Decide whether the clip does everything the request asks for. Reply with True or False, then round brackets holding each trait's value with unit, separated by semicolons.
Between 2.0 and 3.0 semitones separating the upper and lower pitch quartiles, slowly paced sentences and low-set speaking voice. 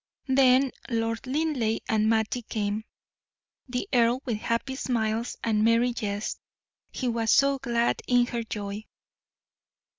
False (2.4 semitones; 125 wpm; 235 Hz)